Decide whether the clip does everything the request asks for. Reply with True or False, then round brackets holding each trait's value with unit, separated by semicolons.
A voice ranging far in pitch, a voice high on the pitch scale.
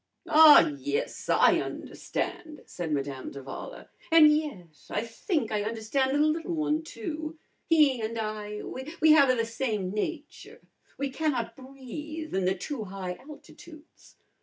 True (6.6 semitones; 265 Hz)